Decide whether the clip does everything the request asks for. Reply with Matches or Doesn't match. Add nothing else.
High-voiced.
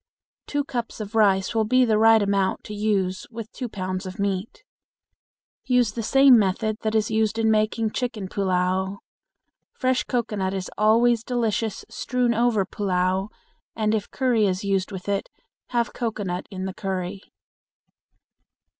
Matches